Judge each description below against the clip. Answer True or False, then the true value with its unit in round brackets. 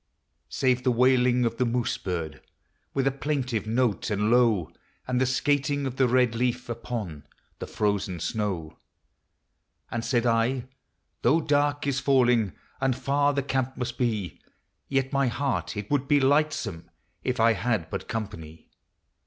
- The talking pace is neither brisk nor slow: True (155 wpm)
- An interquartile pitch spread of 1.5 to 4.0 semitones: True (3.3 semitones)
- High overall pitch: False (125 Hz)